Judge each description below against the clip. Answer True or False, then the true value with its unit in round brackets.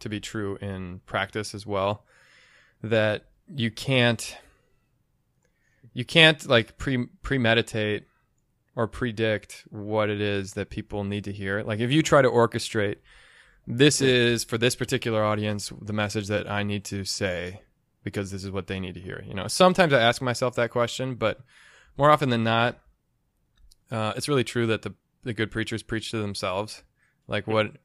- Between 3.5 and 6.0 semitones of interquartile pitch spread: False (2.8 semitones)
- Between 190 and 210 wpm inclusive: False (170 wpm)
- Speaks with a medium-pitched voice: False (110 Hz)